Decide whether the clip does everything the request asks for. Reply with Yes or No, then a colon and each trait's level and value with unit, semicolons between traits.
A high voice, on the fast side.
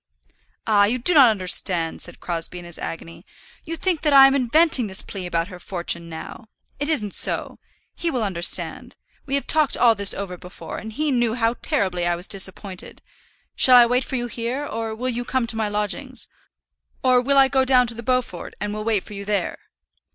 Yes: high, 225 Hz; fast, 210 wpm